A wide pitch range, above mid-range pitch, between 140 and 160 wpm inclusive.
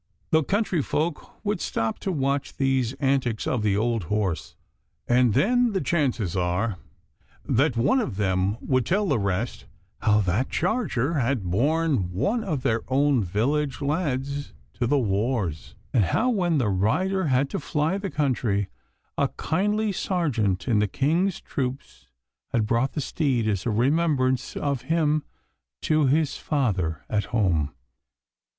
No: wide, 6.6 semitones; low, 130 Hz; average, 150 wpm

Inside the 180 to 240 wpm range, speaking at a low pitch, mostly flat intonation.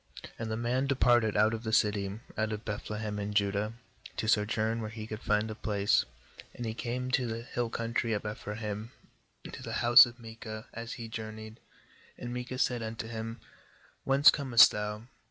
Yes: average, 190 wpm; low, 110 Hz; narrow, 1.8 semitones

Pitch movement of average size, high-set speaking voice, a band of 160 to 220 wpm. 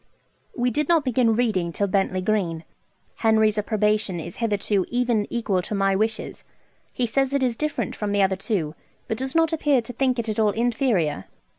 Yes: average, 4.0 semitones; high, 220 Hz; average, 185 wpm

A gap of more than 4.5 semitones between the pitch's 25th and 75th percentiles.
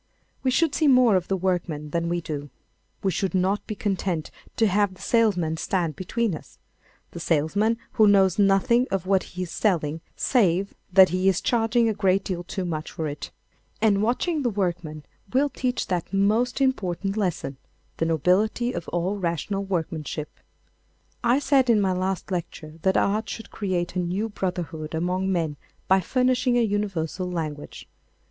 No: average, 4.1 semitones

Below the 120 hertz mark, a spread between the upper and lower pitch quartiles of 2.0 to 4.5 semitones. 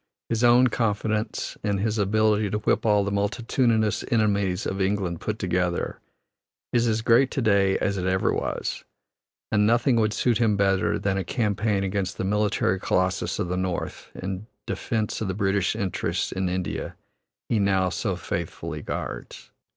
Yes: low, 100 Hz; narrow, 2.5 semitones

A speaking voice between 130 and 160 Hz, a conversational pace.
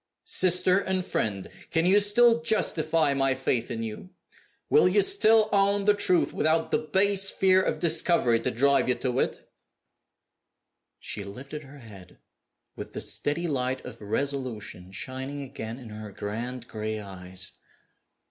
Yes: medium, 140 Hz; average, 150 wpm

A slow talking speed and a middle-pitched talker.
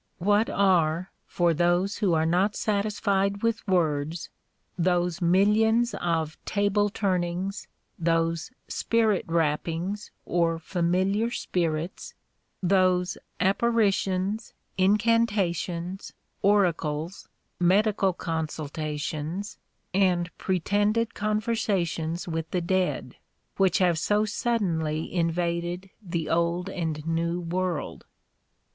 Yes: slow, 95 wpm; medium, 180 Hz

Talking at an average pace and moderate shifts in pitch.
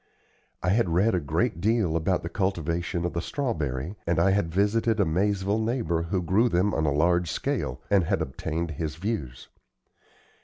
Yes: average, 180 wpm; average, 3.8 semitones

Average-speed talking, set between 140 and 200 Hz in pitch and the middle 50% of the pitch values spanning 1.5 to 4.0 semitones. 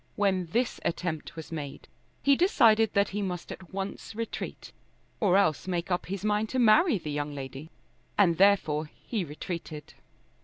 No: average, 160 wpm; medium, 185 Hz; average, 4.7 semitones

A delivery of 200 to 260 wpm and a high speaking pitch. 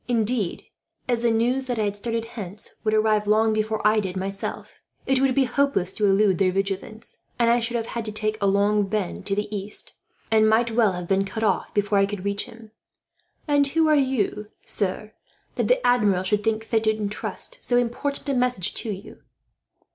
Yes: fast, 205 wpm; high, 215 Hz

